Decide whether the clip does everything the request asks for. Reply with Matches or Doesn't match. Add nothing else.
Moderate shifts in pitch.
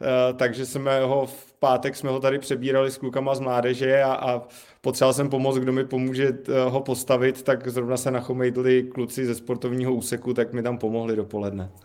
Doesn't match